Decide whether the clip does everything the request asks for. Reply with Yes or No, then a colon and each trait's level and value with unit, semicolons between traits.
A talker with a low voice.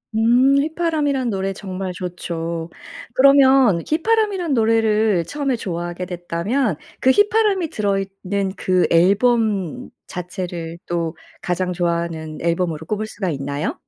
No: high, 195 Hz